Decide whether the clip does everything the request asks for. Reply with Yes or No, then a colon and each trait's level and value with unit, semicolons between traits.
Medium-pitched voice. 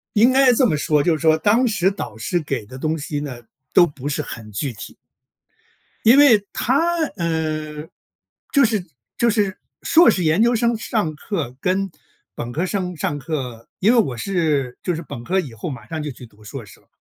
Yes: medium, 160 Hz